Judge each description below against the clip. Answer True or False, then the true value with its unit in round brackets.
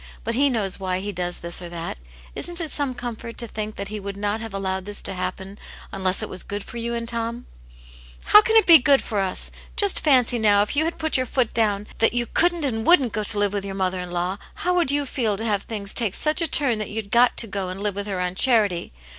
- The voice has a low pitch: False (215 Hz)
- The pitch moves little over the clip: False (4.2 semitones)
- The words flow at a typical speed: False (270 wpm)